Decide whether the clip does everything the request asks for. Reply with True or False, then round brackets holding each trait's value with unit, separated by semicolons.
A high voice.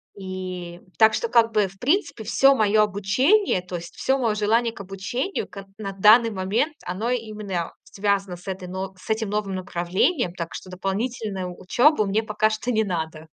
True (205 Hz)